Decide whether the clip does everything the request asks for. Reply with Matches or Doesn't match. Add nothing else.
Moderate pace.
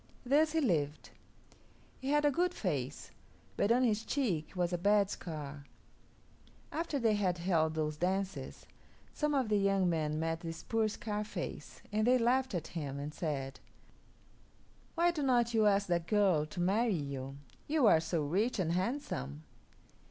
Matches